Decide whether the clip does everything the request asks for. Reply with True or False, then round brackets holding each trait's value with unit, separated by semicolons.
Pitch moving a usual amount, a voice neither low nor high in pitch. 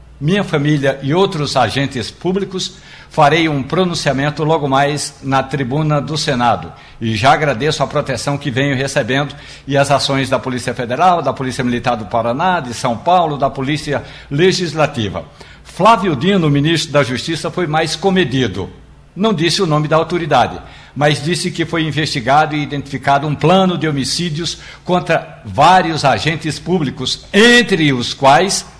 True (3.8 semitones; 145 Hz)